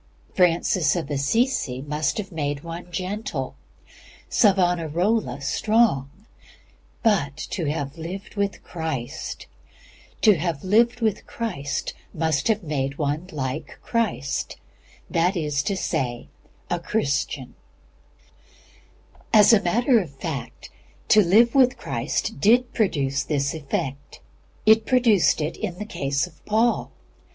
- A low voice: No, medium, 170 Hz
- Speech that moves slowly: Yes, slow, 105 wpm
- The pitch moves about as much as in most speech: No, wide, 6.9 semitones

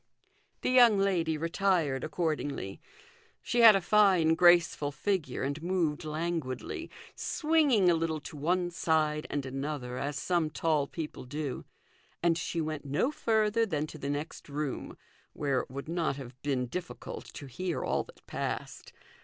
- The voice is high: No, medium, 160 Hz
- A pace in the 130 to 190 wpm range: Yes, average, 155 wpm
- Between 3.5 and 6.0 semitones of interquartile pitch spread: Yes, average, 4.1 semitones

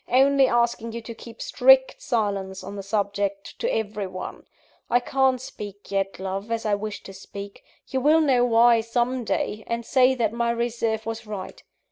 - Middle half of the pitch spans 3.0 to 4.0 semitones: Yes, average, 3.3 semitones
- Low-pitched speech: No, high, 230 Hz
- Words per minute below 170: No, average, 180 wpm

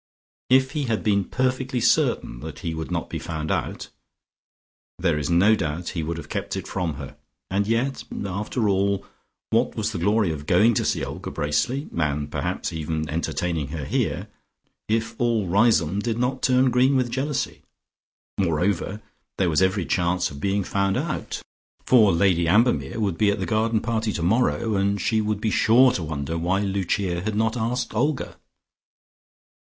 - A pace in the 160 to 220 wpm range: Yes, average, 170 wpm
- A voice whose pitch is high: No, low, 100 Hz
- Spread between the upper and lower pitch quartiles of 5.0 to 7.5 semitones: Yes, average, 5.3 semitones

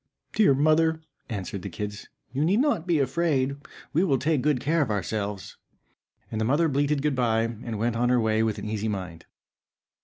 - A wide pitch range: Yes, wide, 5.7 semitones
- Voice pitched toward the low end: Yes, low, 125 Hz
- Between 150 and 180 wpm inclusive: No, average, 190 wpm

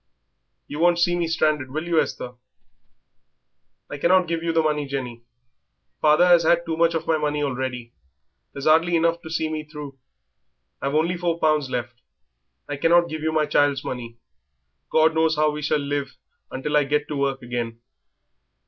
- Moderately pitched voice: Yes, medium, 150 Hz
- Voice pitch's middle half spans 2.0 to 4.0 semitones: Yes, average, 2.9 semitones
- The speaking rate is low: No, average, 180 wpm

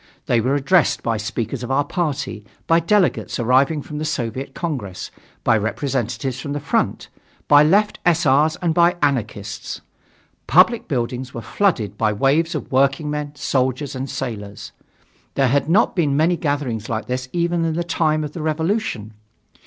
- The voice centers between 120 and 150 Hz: Yes, medium, 140 Hz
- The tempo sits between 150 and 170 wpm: Yes, average, 160 wpm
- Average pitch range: Yes, average, 4.8 semitones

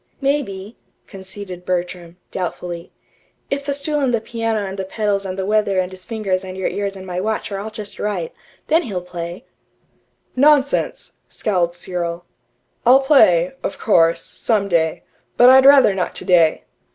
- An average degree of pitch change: Yes, average, 4.1 semitones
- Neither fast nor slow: Yes, average, 165 wpm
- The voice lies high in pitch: Yes, high, 195 Hz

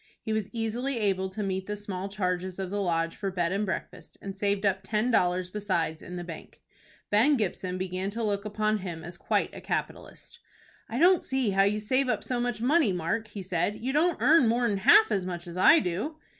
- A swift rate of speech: Yes, fast, 215 wpm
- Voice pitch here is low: No, high, 200 Hz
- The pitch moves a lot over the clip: No, average, 3.6 semitones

